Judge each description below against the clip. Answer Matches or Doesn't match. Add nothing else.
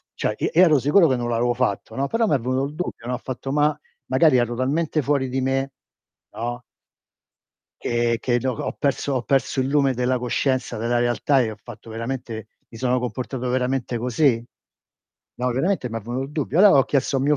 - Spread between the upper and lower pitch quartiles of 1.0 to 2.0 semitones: Doesn't match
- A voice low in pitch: Matches